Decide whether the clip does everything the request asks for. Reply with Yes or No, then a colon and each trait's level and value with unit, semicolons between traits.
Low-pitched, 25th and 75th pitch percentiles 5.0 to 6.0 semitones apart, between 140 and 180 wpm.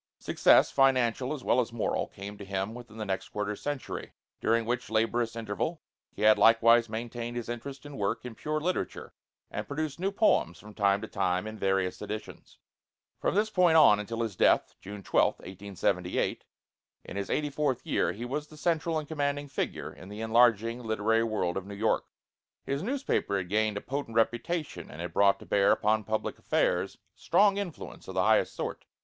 No: low, 115 Hz; wide, 5.6 semitones; average, 190 wpm